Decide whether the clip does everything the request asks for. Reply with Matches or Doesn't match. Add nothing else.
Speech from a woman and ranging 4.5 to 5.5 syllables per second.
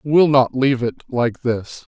Doesn't match